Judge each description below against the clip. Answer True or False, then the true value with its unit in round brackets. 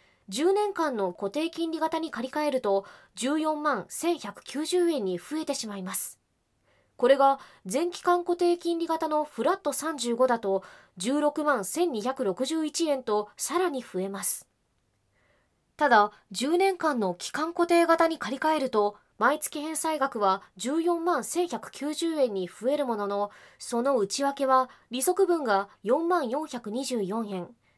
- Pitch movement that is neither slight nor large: False (6.9 semitones)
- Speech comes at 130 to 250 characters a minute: True (210 characters per minute)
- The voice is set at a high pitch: True (280 Hz)